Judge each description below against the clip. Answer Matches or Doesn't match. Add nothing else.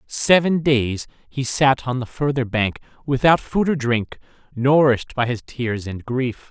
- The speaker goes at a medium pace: Matches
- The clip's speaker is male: Matches